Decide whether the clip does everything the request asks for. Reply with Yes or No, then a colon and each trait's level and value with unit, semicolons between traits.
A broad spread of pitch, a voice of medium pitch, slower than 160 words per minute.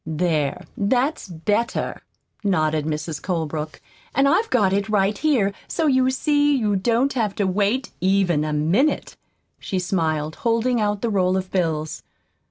No: wide, 6.7 semitones; high, 195 Hz; average, 150 wpm